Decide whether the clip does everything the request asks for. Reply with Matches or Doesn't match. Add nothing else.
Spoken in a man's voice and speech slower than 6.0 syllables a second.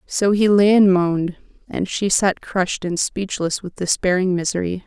Doesn't match